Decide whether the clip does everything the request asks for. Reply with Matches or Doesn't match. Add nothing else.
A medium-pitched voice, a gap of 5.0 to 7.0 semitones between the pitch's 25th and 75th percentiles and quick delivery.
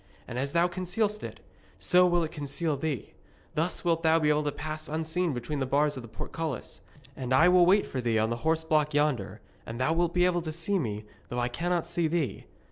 Doesn't match